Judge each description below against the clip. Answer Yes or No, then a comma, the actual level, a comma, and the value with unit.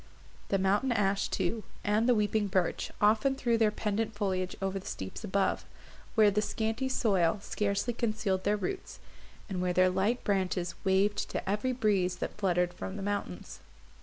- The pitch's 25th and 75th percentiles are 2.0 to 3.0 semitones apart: Yes, narrow, 2.5 semitones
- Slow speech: No, average, 165 wpm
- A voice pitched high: Yes, high, 205 Hz